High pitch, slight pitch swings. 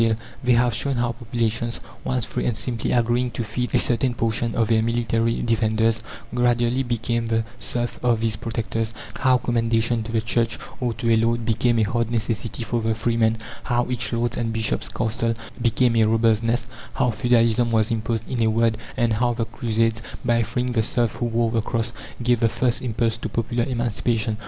No: low, 115 Hz; narrow, 1.1 semitones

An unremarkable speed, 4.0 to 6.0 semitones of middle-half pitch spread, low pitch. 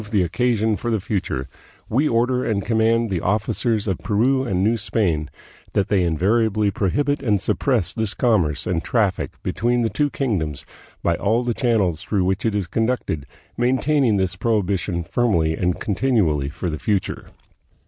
Yes: average, 170 wpm; average, 4.5 semitones; low, 105 Hz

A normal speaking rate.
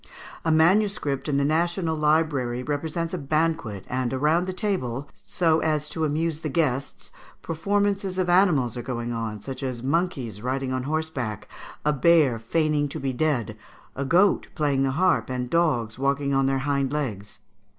Yes: average, 165 wpm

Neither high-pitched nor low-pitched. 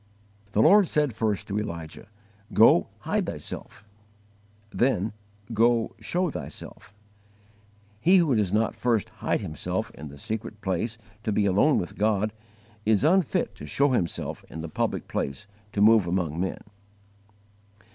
No: low, 105 Hz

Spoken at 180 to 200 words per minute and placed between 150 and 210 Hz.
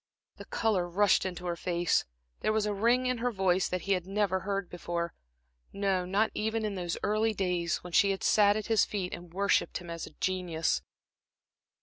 Yes: average, 195 wpm; high, 190 Hz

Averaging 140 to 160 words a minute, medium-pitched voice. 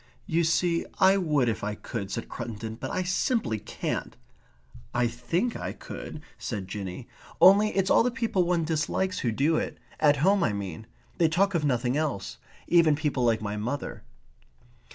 No: average, 175 wpm; medium, 145 Hz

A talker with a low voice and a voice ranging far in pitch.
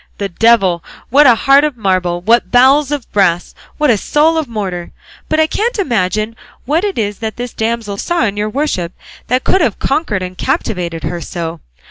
No: high, 225 Hz; wide, 7.3 semitones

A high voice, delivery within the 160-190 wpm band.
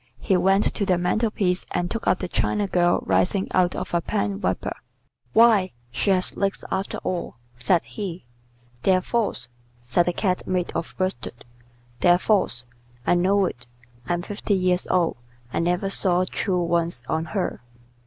No: medium, 180 Hz; average, 165 wpm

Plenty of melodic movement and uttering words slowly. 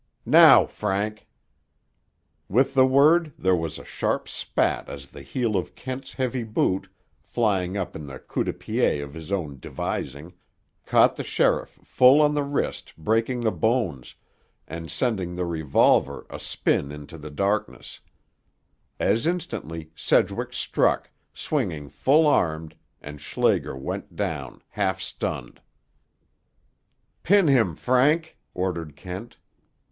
Yes: wide, 8.2 semitones; slow, 130 wpm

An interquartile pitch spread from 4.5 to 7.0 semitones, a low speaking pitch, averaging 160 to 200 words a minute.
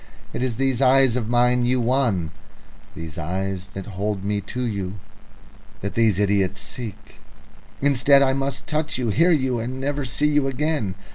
Yes: average, 5.2 semitones; low, 120 Hz; average, 165 wpm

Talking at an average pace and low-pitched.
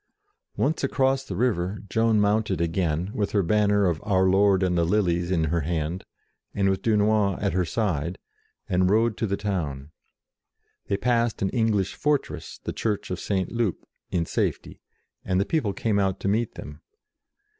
Yes: average, 170 wpm; low, 100 Hz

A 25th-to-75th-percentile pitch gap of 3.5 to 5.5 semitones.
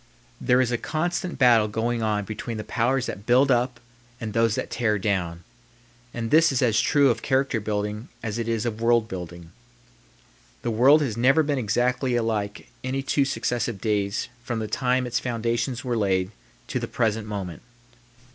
No: average, 3.0 semitones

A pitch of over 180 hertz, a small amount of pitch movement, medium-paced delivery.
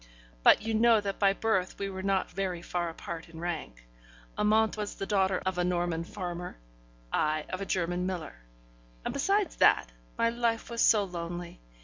No: high, 190 Hz; average, 3.4 semitones; average, 175 wpm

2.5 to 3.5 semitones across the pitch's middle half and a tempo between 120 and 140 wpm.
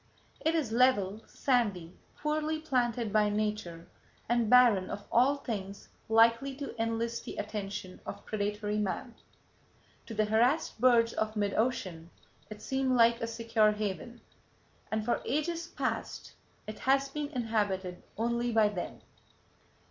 Yes: average, 3.1 semitones; slow, 135 wpm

